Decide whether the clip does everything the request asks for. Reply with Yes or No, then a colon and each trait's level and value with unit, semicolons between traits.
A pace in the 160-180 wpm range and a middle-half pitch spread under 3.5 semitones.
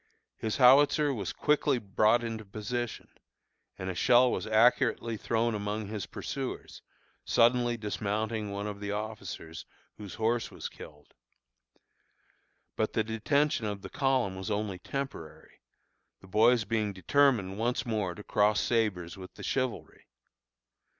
No: slow, 135 wpm; average, 2.9 semitones